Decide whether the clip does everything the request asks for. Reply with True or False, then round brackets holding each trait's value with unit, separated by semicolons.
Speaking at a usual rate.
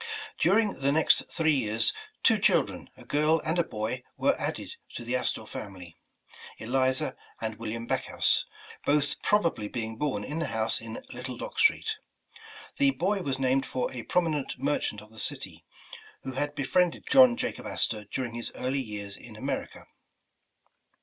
True (165 wpm)